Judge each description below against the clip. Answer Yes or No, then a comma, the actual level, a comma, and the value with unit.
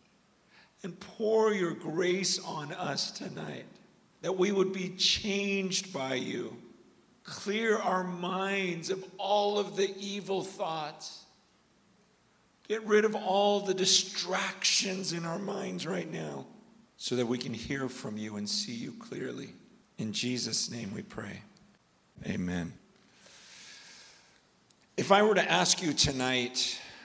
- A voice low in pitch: No, medium, 185 Hz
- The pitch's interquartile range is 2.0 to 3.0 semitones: No, average, 4.2 semitones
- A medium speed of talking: No, slow, 130 wpm